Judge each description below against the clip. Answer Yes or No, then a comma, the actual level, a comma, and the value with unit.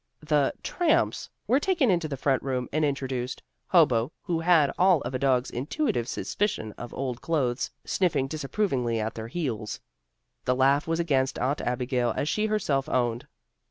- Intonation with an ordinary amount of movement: Yes, average, 5.0 semitones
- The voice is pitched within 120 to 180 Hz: Yes, low, 135 Hz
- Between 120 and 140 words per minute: No, average, 160 wpm